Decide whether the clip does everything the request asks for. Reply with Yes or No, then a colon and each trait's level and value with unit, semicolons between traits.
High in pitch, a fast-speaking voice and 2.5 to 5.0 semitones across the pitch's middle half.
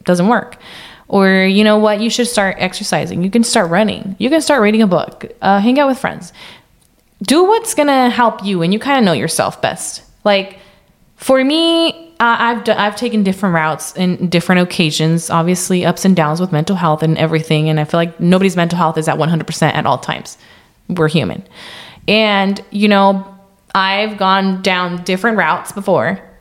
No: high, 195 Hz; average, 190 wpm; average, 4.0 semitones